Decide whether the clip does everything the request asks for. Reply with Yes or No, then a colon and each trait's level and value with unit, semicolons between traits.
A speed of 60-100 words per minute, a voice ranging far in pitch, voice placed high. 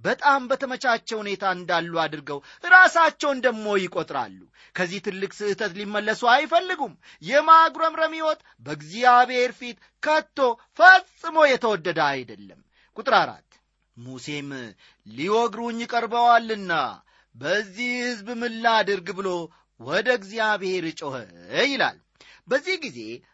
Yes: average, 95 wpm; wide, 6.2 semitones; high, 225 Hz